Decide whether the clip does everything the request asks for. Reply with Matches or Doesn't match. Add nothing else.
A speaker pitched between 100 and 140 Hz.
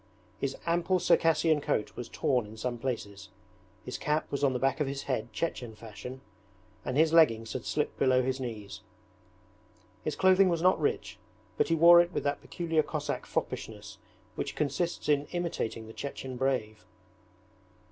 Matches